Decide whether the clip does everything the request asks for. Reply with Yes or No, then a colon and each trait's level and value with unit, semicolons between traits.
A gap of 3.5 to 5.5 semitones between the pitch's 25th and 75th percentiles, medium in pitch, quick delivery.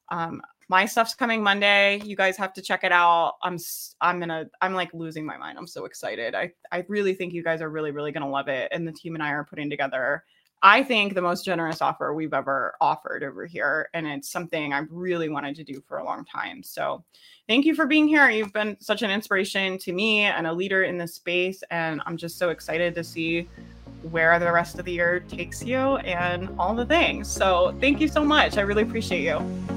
Yes: average, 3.8 semitones; medium, 180 Hz; fast, 230 wpm